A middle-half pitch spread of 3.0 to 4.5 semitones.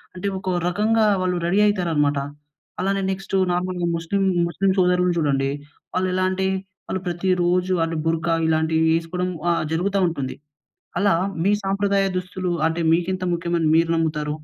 No: narrow, 2.4 semitones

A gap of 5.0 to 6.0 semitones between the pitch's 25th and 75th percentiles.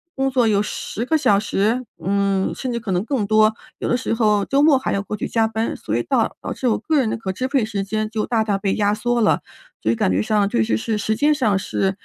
No: average, 3.3 semitones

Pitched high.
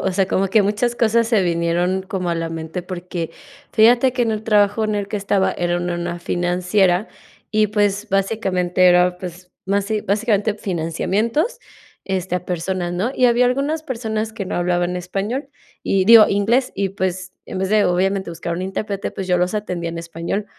Yes: high, 195 Hz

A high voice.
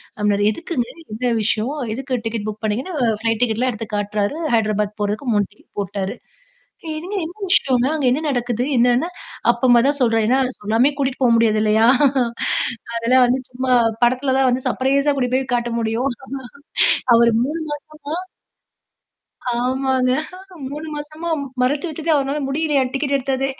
Yes: very high, 255 Hz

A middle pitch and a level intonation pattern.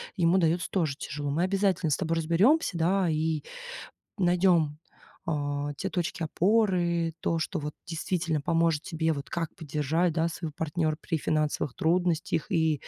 Yes: medium, 165 Hz; narrow, 2.3 semitones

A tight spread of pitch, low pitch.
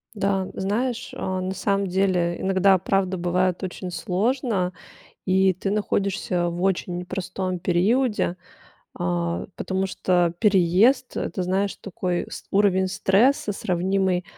No: narrow, 1.8 semitones; high, 190 Hz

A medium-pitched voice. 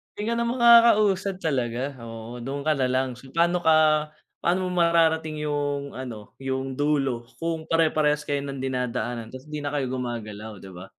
Yes: medium, 145 Hz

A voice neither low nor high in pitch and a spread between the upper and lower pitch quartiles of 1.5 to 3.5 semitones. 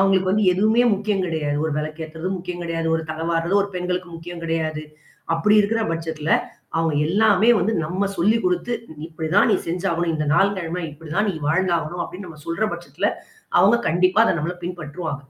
Yes: medium, 175 Hz; average, 2.9 semitones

